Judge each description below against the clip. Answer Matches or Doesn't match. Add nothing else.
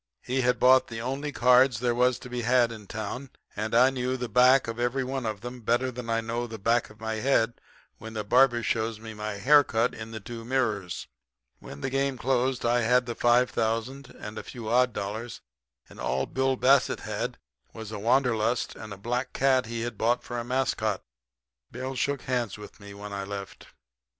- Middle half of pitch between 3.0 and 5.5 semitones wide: Doesn't match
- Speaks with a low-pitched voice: Matches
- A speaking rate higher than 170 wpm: Matches